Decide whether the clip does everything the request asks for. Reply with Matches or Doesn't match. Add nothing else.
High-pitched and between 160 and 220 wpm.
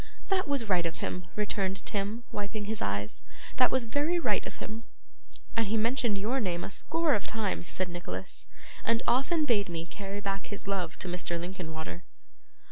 Matches